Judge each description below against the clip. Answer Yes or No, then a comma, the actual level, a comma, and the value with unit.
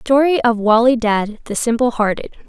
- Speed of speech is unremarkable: Yes, average, 170 wpm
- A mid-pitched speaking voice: No, high, 235 Hz